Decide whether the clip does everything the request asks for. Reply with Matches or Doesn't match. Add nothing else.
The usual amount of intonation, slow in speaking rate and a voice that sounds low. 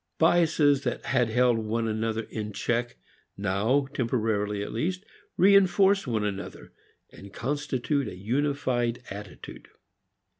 Matches